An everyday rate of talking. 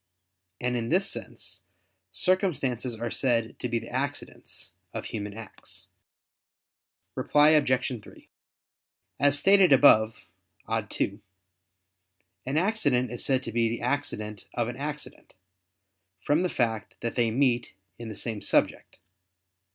No: slow, 130 wpm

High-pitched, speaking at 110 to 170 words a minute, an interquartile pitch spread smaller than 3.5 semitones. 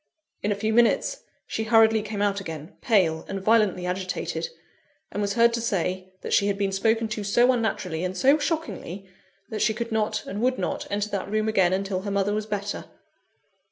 No: high, 205 Hz; average, 195 wpm; narrow, 2.4 semitones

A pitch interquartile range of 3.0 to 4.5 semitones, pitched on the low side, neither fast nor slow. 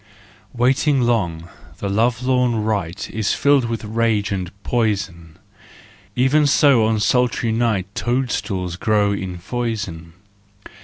No: average, 4.0 semitones; low, 110 Hz; slow, 110 wpm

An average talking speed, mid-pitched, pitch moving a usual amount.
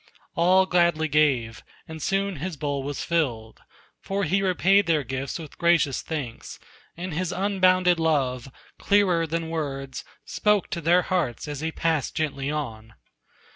Yes: average, 145 wpm; medium, 160 Hz; average, 4.5 semitones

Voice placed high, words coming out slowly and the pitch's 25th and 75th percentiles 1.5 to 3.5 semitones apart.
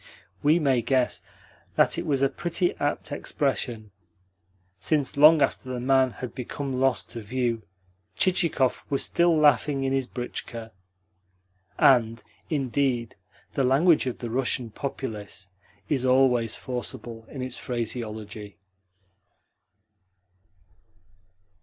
No: low, 130 Hz; slow, 115 wpm; average, 3.1 semitones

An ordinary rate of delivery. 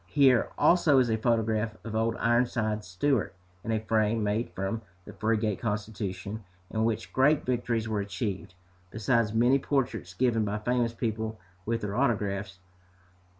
Yes: average, 150 wpm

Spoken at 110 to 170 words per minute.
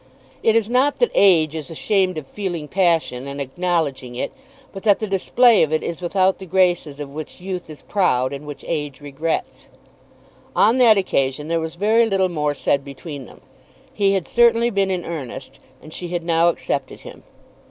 No: average, 185 wpm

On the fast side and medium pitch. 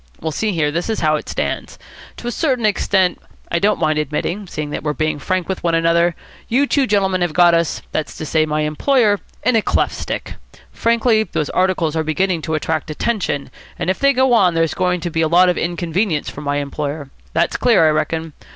Yes: fast, 215 wpm; medium, 170 Hz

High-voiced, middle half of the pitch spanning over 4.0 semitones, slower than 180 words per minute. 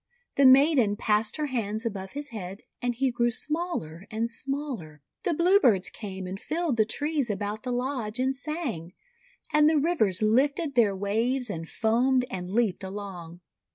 Yes: high, 235 Hz; wide, 5.6 semitones; average, 160 wpm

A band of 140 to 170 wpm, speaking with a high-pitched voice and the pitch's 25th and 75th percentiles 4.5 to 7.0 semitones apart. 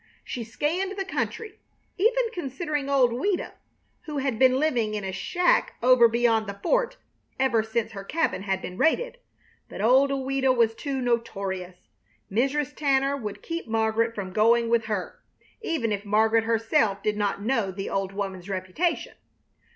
Yes: average, 160 wpm; high, 235 Hz; average, 5.3 semitones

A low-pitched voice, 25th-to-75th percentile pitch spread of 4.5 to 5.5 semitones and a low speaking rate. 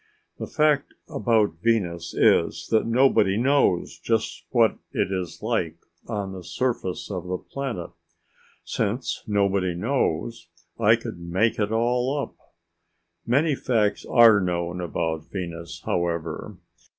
Yes: low, 105 Hz; average, 5.0 semitones; slow, 125 wpm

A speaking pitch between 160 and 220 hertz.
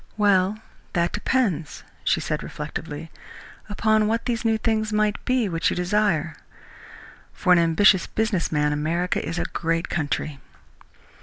Yes: medium, 185 Hz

